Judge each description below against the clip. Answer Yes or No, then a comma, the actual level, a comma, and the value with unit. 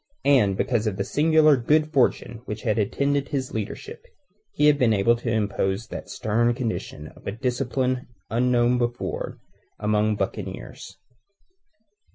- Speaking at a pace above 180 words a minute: No, average, 140 wpm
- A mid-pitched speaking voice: No, low, 120 Hz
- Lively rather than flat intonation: No, average, 3.6 semitones